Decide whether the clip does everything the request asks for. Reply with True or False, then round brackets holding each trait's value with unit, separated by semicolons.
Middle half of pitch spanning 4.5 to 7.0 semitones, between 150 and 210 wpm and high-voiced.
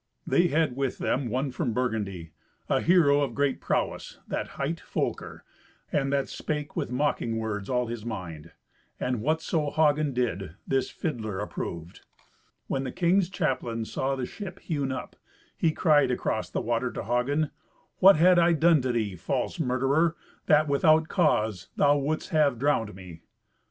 False (5.2 semitones; 160 wpm; 135 Hz)